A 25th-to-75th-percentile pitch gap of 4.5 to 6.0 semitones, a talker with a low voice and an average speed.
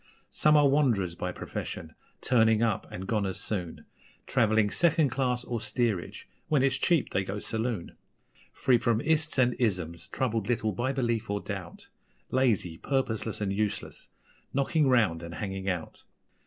Yes: average, 5.1 semitones; low, 110 Hz; average, 155 wpm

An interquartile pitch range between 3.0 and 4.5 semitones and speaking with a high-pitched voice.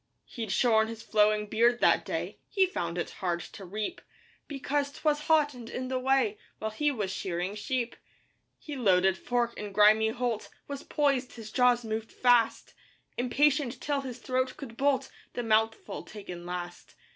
Yes: average, 4.1 semitones; high, 235 Hz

